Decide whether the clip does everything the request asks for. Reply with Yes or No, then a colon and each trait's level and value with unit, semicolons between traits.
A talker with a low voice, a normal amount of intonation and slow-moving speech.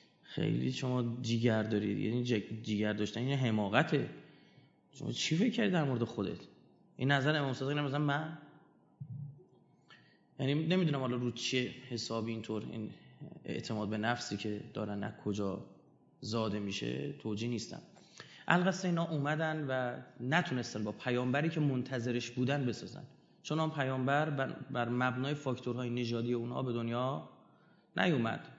No: low, 125 Hz; average, 4.1 semitones; average, 130 wpm